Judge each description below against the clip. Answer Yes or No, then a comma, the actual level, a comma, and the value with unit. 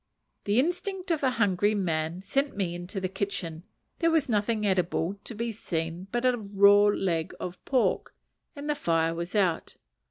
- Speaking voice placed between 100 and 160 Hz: No, high, 200 Hz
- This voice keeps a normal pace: Yes, average, 170 wpm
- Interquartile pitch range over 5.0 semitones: Yes, wide, 5.5 semitones